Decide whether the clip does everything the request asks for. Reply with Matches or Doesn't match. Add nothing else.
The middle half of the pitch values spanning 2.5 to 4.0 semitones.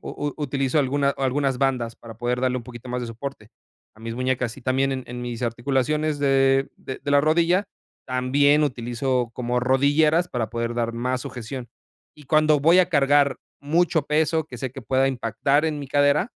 Matches